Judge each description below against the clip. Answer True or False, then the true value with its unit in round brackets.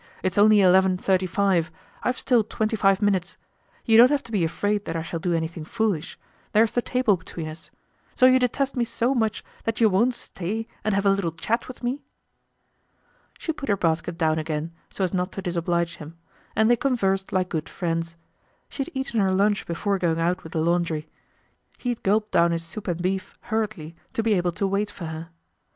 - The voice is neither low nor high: False (195 Hz)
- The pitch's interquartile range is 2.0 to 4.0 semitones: False (4.6 semitones)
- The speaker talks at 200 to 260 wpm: True (205 wpm)